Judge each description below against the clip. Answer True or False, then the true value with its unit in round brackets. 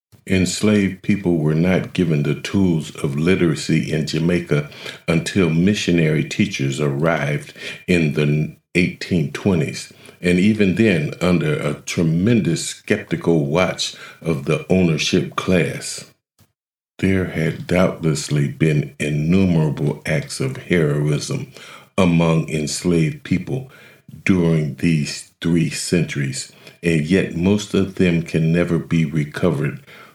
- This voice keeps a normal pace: False (105 wpm)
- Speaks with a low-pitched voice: True (85 Hz)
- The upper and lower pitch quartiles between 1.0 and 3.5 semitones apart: True (2.9 semitones)